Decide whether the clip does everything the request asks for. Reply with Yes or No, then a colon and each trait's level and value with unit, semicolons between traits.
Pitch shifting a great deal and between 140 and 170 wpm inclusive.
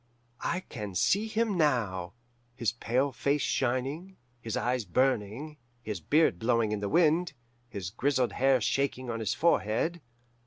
Yes: wide, 5.8 semitones; average, 145 wpm